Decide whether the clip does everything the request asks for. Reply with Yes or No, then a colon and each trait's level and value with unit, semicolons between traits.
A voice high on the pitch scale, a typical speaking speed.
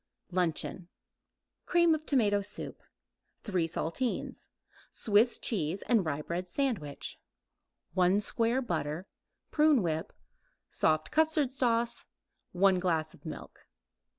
No: high, 200 Hz; slow, 100 wpm